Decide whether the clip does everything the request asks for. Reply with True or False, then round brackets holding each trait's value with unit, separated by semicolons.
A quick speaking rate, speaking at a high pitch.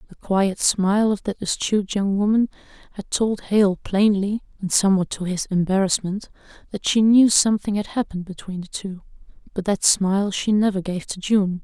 False (175 wpm; 195 Hz)